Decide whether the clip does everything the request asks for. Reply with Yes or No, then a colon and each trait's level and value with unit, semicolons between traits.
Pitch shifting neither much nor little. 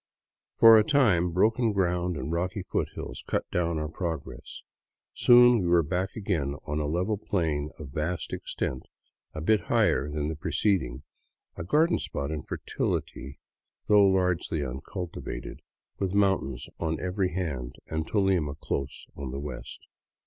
Yes: average, 4.6 semitones